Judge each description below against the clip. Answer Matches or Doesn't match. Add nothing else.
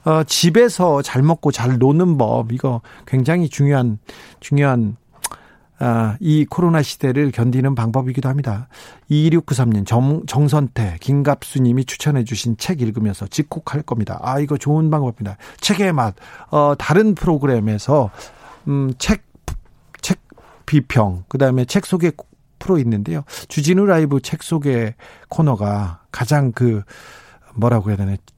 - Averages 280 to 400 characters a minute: Doesn't match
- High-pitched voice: Doesn't match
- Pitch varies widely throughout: Doesn't match